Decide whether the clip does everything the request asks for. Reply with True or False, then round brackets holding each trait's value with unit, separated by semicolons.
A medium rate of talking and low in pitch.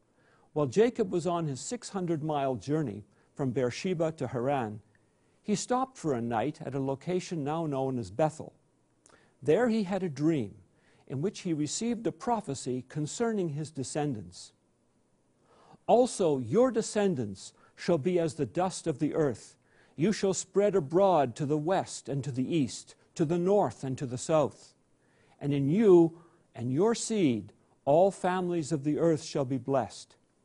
False (160 wpm; 155 Hz)